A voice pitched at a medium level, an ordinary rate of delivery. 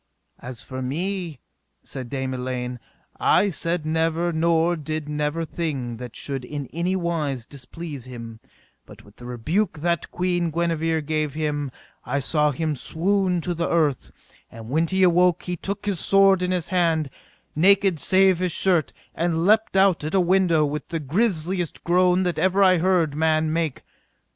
Yes: medium, 165 Hz; average, 165 wpm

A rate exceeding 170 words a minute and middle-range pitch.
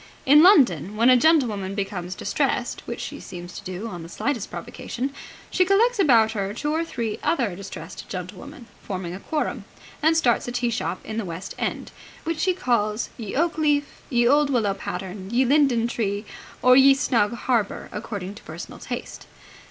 No: average, 180 wpm; high, 235 Hz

